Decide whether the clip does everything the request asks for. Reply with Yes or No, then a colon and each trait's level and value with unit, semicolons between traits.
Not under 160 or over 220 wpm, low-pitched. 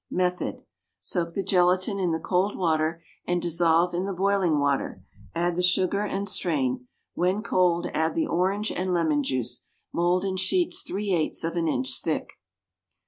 No: average, 165 wpm; medium, 180 Hz